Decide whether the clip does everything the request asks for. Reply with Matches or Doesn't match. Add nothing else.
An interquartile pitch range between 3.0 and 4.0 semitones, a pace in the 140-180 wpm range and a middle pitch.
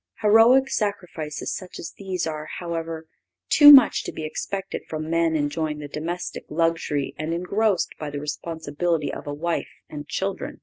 Matches